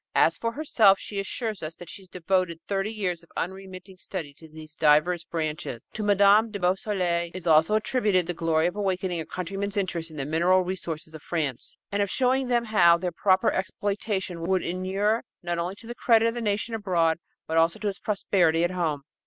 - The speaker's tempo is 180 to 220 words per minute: Yes, average, 200 wpm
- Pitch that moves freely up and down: No, average, 3.5 semitones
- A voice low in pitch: No, medium, 185 Hz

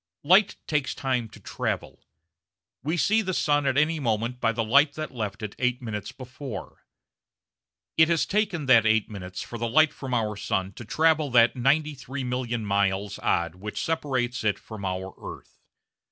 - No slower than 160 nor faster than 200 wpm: Yes, average, 170 wpm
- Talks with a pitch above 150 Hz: No, low, 125 Hz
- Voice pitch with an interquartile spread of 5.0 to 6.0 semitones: Yes, average, 5.3 semitones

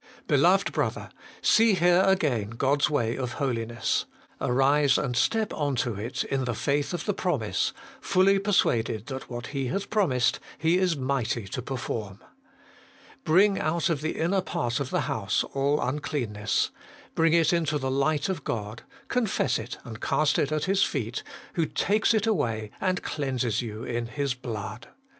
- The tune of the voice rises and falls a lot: Yes, wide, 6.1 semitones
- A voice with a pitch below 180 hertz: Yes, medium, 140 Hz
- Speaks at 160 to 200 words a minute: Yes, average, 165 wpm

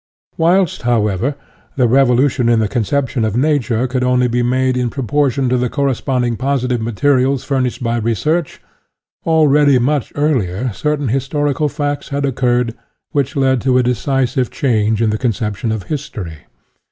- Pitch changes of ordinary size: Yes, average, 3.1 semitones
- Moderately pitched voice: No, low, 130 Hz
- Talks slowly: No, average, 155 wpm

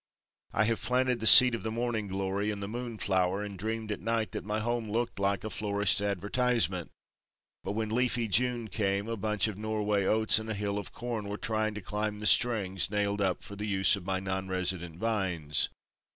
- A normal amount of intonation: No, narrow, 2.3 semitones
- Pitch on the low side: Yes, low, 105 Hz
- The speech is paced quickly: Yes, fast, 210 wpm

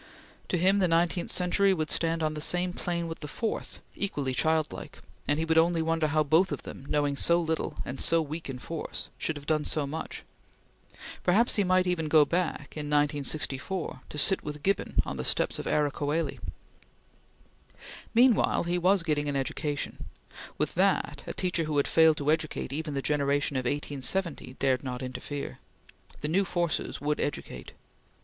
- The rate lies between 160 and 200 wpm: Yes, average, 175 wpm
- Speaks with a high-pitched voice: No, medium, 155 Hz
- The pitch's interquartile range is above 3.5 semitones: No, average, 3.0 semitones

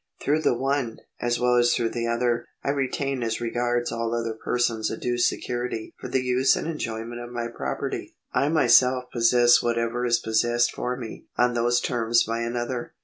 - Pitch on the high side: No, low, 120 Hz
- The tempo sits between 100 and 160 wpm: No, average, 185 wpm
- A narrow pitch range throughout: Yes, narrow, 1.1 semitones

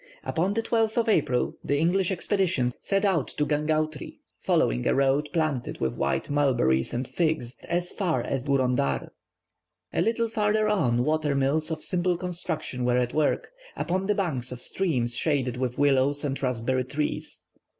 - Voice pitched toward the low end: No, medium, 150 Hz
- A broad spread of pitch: Yes, wide, 5.8 semitones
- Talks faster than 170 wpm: No, average, 160 wpm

